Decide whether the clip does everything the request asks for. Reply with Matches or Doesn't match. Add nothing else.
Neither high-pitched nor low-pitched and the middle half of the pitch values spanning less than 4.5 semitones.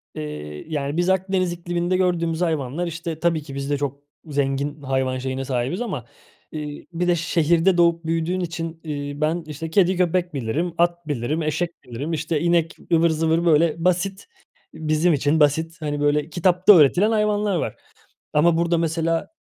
Matches